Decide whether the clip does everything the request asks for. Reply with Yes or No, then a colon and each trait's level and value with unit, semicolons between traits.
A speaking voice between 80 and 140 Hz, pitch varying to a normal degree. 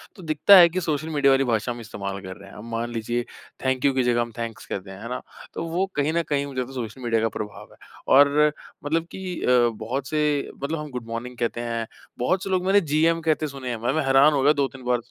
Yes: low, 135 Hz; average, 4.7 semitones